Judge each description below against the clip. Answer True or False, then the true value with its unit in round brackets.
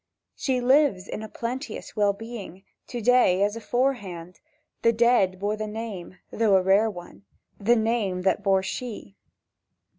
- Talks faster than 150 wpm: False (145 wpm)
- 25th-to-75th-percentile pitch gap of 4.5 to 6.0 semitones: False (3.8 semitones)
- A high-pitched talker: True (210 Hz)